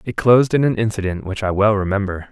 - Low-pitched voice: Yes, low, 105 Hz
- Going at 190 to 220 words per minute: No, fast, 235 wpm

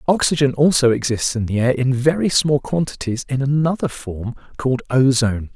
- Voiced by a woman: No, male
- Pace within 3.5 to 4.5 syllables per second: No, 5.4 syllables/s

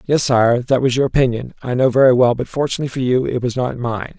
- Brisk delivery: Yes, fast, 260 wpm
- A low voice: Yes, low, 125 Hz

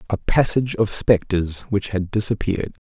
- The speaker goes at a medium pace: Yes, average, 145 wpm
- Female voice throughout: No, male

